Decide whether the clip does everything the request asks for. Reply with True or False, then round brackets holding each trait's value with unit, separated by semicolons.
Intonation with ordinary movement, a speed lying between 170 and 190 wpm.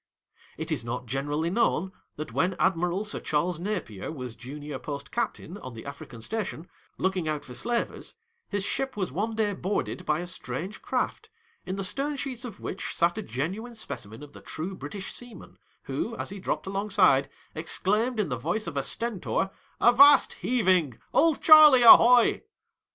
False (7.0 semitones; 175 wpm)